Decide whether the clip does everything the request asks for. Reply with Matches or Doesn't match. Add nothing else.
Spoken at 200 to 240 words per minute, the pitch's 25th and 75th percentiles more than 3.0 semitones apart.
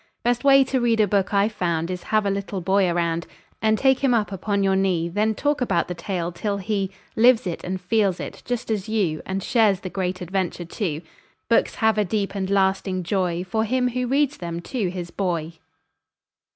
Matches